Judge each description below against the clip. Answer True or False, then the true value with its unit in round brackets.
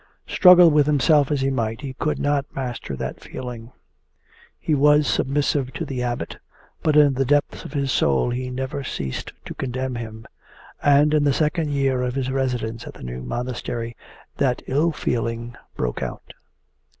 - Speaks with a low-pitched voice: True (130 Hz)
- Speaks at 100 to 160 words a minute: False (170 wpm)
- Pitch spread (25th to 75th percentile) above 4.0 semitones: False (3.2 semitones)